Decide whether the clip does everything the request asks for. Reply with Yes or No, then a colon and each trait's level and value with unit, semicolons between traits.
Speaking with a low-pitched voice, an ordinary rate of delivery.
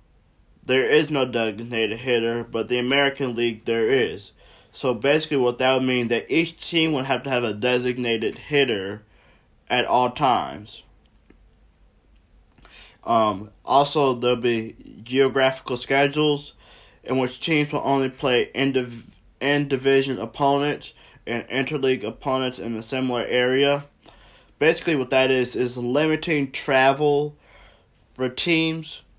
No: low, 130 Hz; slow, 130 wpm